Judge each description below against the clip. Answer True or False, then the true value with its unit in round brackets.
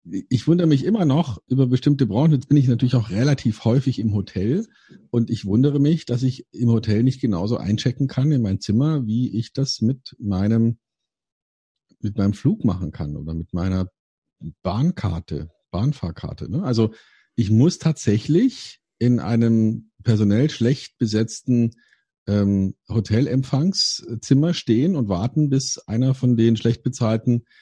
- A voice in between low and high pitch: False (120 Hz)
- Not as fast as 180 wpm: True (145 wpm)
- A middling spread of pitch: True (4.0 semitones)